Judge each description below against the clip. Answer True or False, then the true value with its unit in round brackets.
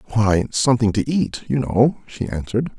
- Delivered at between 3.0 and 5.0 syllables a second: False (5.3 syllables/s)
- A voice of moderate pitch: False (115 Hz)